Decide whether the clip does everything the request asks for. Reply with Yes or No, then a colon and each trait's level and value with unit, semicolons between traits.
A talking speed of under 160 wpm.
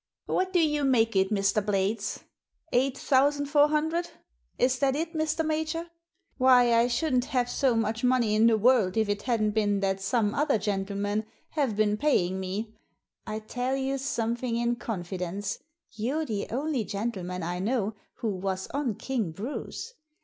No: average, 165 wpm